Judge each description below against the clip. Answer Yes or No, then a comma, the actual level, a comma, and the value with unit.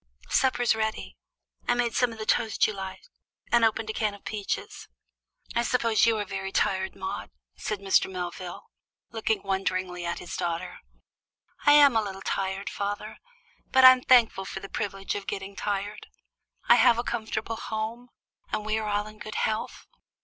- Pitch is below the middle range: No, high, 215 Hz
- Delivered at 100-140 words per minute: No, average, 170 wpm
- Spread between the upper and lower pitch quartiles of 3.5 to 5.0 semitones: No, average, 2.8 semitones